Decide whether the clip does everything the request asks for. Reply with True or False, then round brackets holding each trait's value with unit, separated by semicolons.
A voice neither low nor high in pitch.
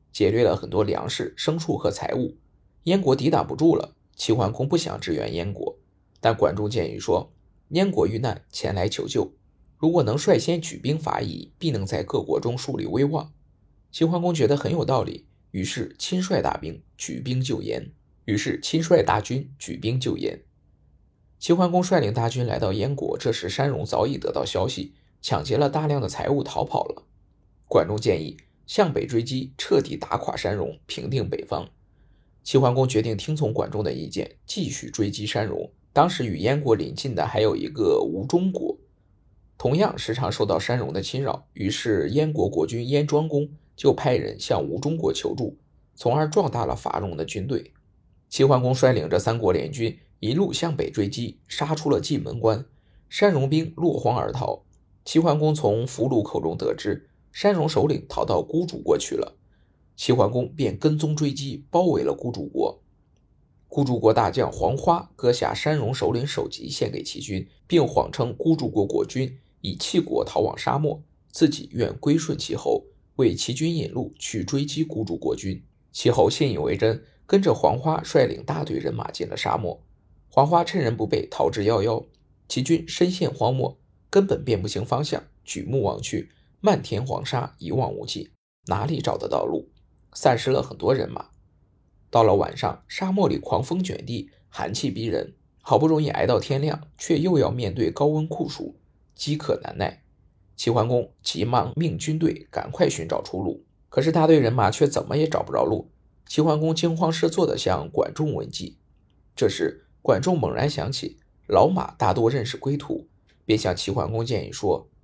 True (145 Hz)